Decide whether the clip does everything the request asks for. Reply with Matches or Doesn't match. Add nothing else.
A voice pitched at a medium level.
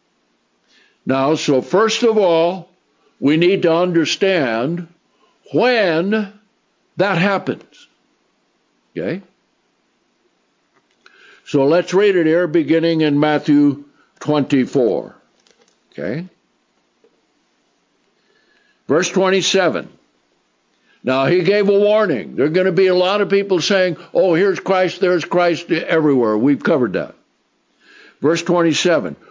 Matches